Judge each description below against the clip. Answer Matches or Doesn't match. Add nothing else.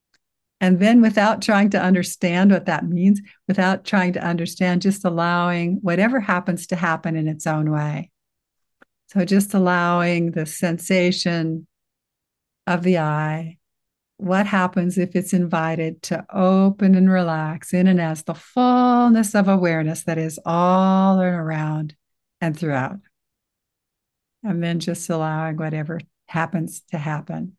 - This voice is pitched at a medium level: Matches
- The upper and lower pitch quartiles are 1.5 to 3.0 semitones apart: Matches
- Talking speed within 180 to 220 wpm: Doesn't match